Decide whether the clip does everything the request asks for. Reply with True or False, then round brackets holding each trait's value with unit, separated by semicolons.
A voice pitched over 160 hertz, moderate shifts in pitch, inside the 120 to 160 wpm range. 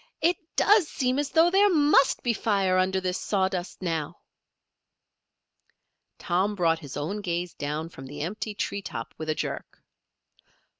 False (190 Hz; 7.1 semitones; 150 wpm)